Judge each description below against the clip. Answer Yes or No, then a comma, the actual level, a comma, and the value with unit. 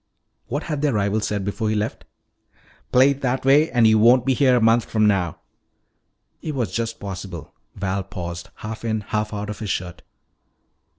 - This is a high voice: No, low, 110 Hz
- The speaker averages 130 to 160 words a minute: No, average, 185 wpm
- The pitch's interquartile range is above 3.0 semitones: Yes, average, 3.8 semitones